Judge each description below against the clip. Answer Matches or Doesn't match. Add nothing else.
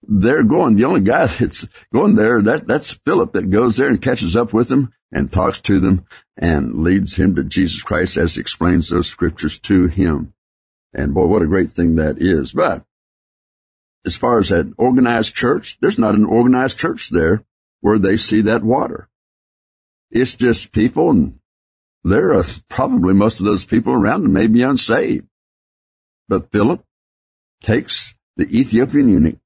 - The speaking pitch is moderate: Doesn't match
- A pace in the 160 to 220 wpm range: Matches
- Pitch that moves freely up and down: Matches